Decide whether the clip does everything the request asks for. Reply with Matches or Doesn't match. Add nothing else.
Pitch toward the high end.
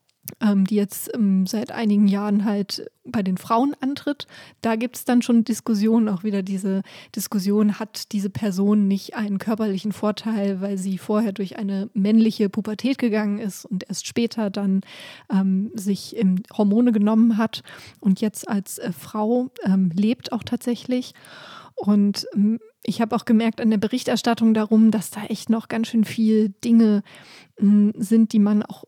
Matches